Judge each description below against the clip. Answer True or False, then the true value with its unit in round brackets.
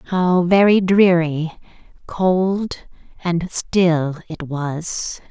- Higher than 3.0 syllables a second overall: False (2.4 syllables/s)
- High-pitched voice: False (175 Hz)